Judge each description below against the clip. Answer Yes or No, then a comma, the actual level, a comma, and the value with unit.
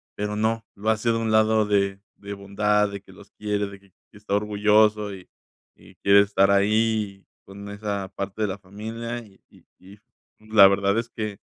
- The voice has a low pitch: Yes, low, 105 Hz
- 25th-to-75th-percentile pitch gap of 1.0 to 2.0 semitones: Yes, narrow, 1.5 semitones